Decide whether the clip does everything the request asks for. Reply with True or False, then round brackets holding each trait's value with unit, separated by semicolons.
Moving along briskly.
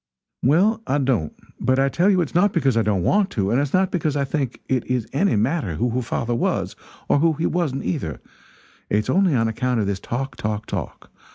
True (220 wpm)